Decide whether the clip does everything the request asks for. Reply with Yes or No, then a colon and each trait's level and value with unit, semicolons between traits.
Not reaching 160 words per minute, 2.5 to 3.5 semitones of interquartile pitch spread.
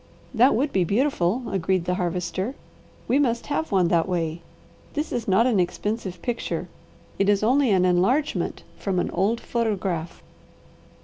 No: average, 150 wpm; average, 5.1 semitones